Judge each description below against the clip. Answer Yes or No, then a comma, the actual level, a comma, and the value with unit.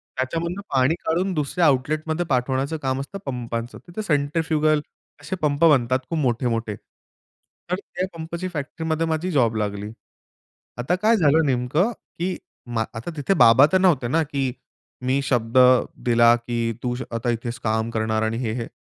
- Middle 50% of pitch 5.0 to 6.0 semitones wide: Yes, wide, 5.5 semitones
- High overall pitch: No, low, 135 Hz